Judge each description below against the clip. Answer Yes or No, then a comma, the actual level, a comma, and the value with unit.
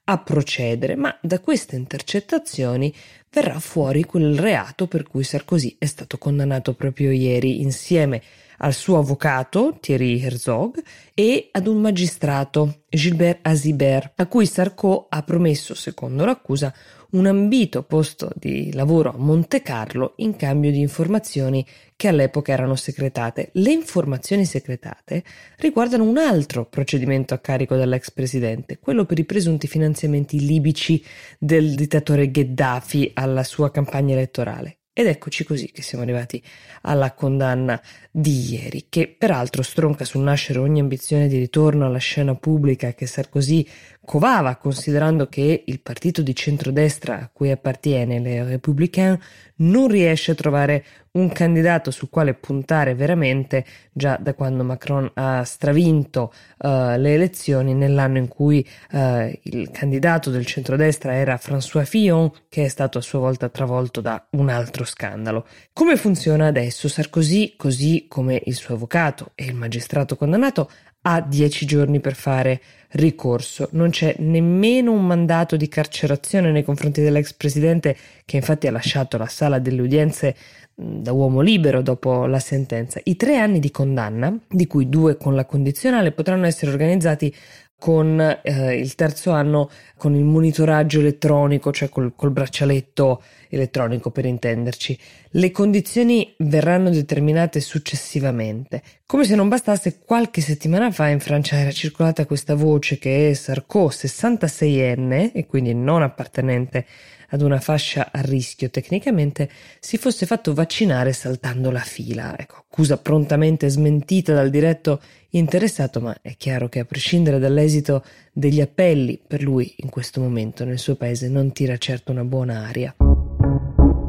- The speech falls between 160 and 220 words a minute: No, average, 145 wpm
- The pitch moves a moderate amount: Yes, average, 3.5 semitones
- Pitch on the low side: No, medium, 145 Hz